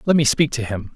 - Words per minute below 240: No, fast, 315 wpm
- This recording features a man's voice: Yes, male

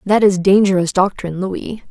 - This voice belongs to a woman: Yes, female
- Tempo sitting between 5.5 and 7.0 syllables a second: No, 5.2 syllables/s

